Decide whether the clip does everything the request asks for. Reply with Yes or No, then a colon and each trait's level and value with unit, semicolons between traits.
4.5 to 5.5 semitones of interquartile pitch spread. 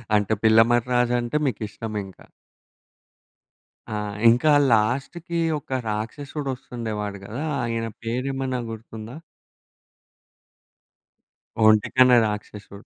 No: average, 3.0 semitones